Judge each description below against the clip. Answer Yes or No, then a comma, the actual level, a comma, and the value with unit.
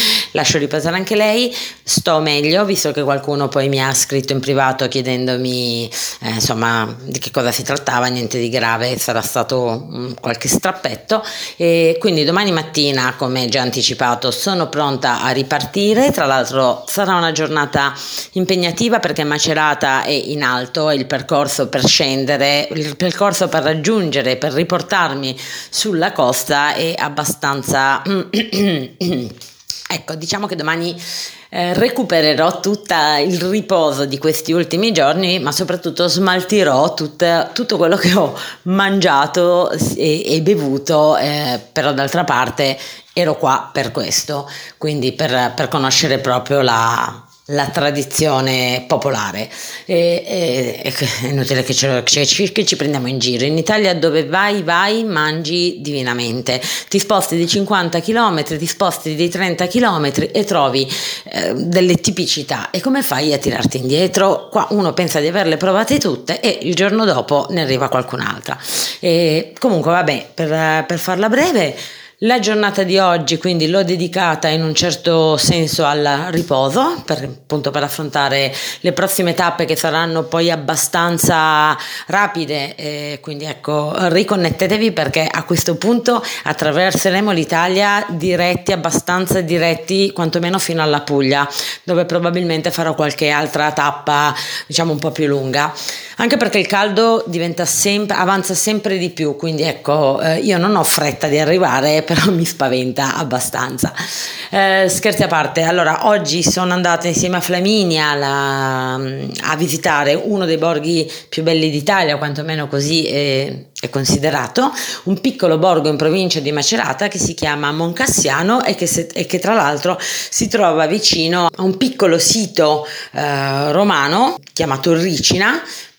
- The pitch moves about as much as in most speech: Yes, average, 4.4 semitones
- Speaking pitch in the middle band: Yes, medium, 160 Hz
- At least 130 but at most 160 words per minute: Yes, average, 145 wpm